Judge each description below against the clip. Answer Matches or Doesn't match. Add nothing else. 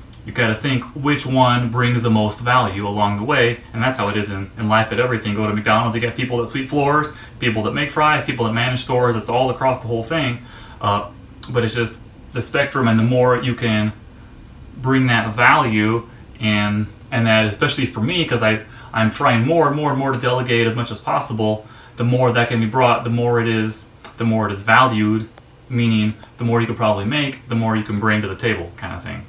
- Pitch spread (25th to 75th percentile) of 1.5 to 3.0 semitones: Matches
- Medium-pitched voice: Doesn't match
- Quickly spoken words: Matches